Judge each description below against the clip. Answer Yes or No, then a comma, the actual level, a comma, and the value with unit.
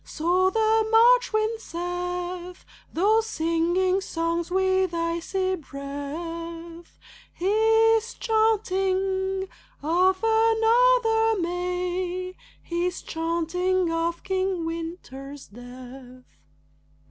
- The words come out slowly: Yes, slow, 75 wpm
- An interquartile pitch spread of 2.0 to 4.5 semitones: Yes, average, 3.6 semitones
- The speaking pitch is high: Yes, very high, 360 Hz